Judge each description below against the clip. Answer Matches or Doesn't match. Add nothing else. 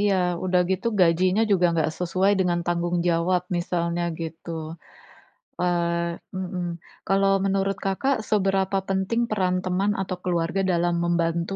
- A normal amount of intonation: Doesn't match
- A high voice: Doesn't match